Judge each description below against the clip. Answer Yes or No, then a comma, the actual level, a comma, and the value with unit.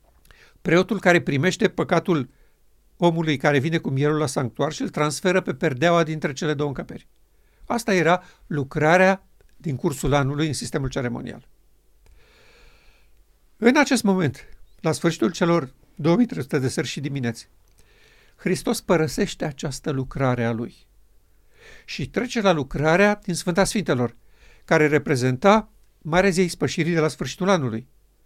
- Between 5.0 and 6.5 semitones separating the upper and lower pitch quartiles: No, average, 4.6 semitones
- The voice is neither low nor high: Yes, medium, 160 Hz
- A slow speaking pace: No, average, 130 wpm